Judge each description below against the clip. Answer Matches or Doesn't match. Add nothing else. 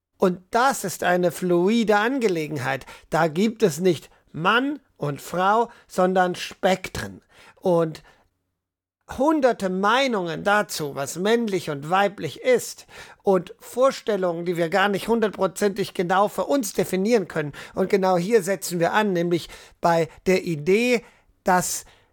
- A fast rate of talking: Doesn't match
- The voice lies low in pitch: Doesn't match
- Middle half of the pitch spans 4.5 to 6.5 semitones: Doesn't match